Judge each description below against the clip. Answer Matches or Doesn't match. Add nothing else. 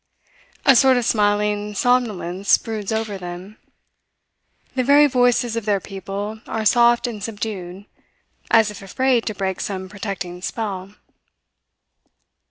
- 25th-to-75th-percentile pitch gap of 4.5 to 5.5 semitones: Doesn't match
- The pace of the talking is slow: Matches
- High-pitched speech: Matches